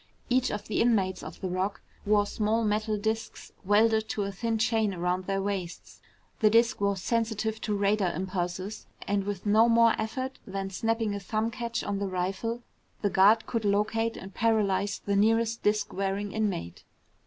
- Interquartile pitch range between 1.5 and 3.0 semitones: Yes, narrow, 2.4 semitones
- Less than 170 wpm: No, average, 175 wpm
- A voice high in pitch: Yes, high, 210 Hz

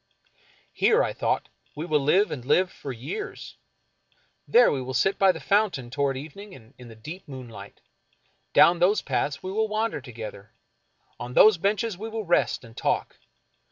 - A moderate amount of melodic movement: No, wide, 7.9 semitones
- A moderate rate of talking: Yes, average, 170 wpm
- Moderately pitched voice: Yes, medium, 150 Hz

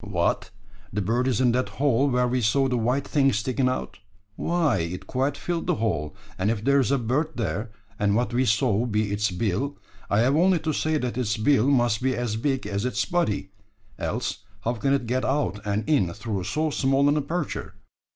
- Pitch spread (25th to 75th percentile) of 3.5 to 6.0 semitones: Yes, average, 4.6 semitones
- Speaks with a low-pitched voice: Yes, low, 125 Hz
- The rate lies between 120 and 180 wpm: No, fast, 205 wpm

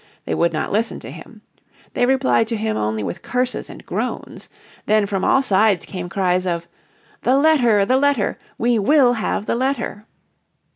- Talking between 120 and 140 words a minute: No, average, 175 wpm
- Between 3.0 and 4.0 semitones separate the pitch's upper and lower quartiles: No, average, 4.8 semitones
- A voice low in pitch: No, high, 220 Hz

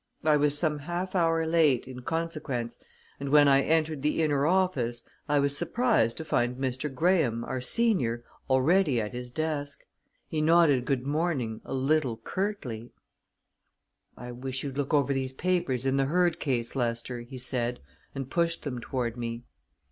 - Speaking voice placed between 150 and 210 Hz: No, medium, 140 Hz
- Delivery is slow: No, average, 165 wpm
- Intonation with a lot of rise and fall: No, average, 4.4 semitones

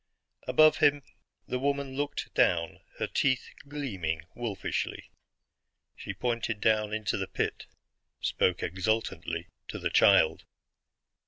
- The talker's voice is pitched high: No, low, 115 Hz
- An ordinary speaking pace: No, slow, 110 wpm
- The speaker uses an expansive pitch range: Yes, wide, 6.4 semitones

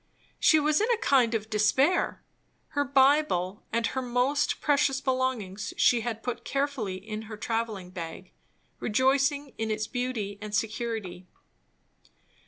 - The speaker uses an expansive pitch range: No, average, 4.4 semitones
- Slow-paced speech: Yes, slow, 130 wpm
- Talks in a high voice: Yes, high, 235 Hz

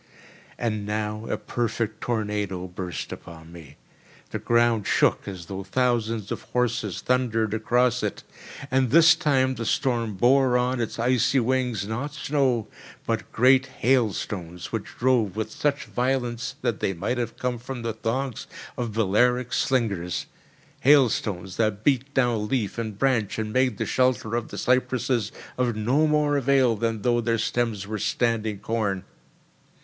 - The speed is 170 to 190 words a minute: No, average, 150 wpm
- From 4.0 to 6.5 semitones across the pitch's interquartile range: No, average, 3.1 semitones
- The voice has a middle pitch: No, low, 115 Hz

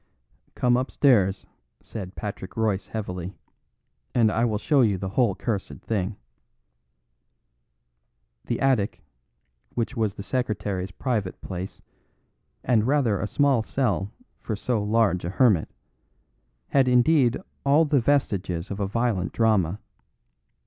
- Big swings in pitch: No, average, 4.3 semitones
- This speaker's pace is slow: Yes, slow, 120 wpm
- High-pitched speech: No, low, 110 Hz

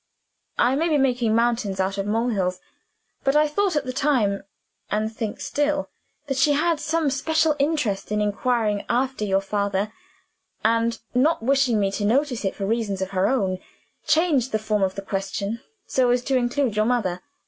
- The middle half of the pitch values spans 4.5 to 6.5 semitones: Yes, average, 5.2 semitones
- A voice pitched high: Yes, high, 235 Hz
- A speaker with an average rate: Yes, average, 180 wpm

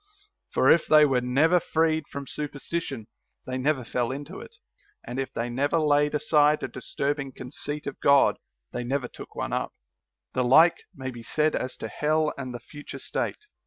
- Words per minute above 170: Yes, average, 180 wpm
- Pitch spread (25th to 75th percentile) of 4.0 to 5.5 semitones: No, average, 2.9 semitones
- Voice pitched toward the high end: No, medium, 140 Hz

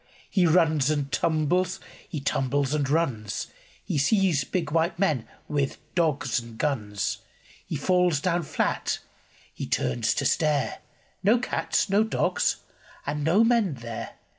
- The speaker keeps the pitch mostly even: No, average, 4.8 semitones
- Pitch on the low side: No, medium, 150 Hz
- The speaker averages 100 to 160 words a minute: Yes, average, 140 wpm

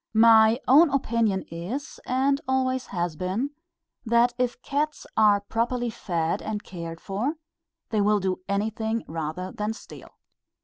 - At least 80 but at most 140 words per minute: Yes, slow, 135 wpm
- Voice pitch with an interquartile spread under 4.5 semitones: No, average, 4.9 semitones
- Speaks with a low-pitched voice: No, high, 220 Hz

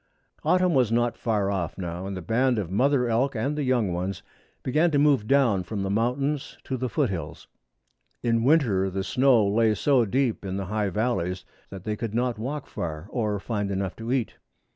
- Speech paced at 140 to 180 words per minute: No, average, 195 wpm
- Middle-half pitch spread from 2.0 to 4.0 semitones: No, average, 4.9 semitones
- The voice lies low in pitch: Yes, low, 115 Hz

